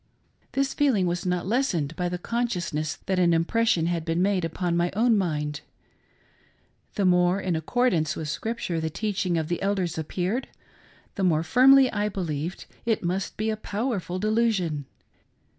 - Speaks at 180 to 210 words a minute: No, average, 160 wpm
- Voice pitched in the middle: Yes, medium, 180 Hz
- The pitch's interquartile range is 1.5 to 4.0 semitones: No, average, 4.6 semitones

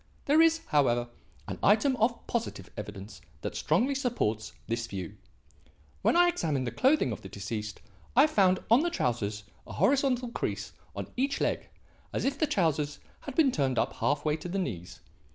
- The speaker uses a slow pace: No, average, 175 wpm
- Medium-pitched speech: Yes, medium, 170 Hz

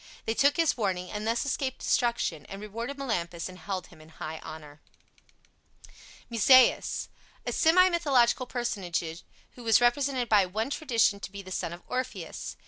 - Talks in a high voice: Yes, high, 225 Hz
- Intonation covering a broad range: Yes, wide, 6.0 semitones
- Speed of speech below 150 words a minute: No, average, 160 wpm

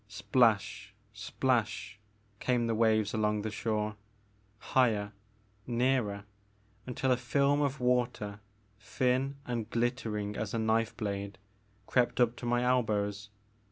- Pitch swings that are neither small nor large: Yes, average, 3.0 semitones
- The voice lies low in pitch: Yes, low, 115 Hz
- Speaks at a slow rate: Yes, slow, 120 wpm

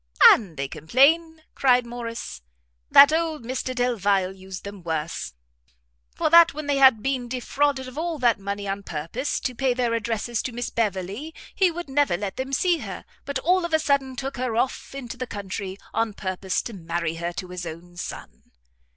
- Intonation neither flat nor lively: No, wide, 6.2 semitones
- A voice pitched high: Yes, high, 240 Hz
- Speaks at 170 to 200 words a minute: Yes, average, 185 wpm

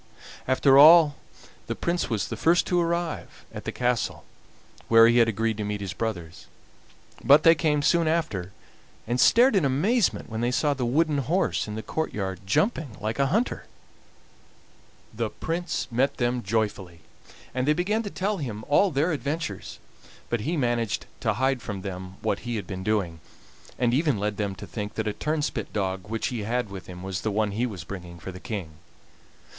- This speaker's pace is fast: No, average, 185 wpm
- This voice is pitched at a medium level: No, low, 120 Hz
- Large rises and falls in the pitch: Yes, wide, 6.9 semitones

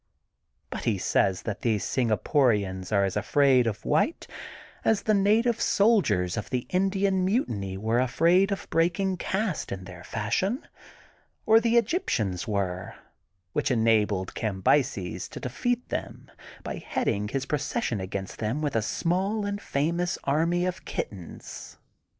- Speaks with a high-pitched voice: No, low, 130 Hz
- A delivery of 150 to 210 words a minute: No, average, 140 wpm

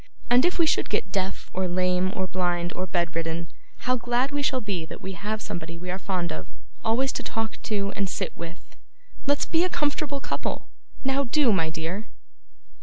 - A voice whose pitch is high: Yes, high, 195 Hz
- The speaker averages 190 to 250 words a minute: Yes, average, 195 wpm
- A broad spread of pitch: Yes, wide, 6.5 semitones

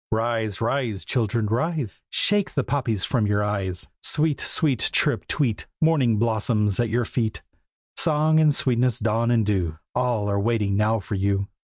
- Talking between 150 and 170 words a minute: Yes, average, 160 wpm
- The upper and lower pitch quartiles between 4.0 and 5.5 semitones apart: No, average, 3.6 semitones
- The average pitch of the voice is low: Yes, low, 115 Hz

